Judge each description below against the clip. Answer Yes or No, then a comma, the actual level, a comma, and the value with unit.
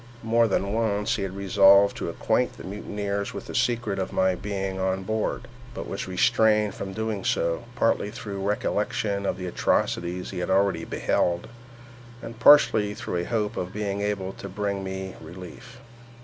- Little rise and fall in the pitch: Yes, narrow, 1.9 semitones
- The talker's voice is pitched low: Yes, low, 100 Hz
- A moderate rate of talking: Yes, average, 175 wpm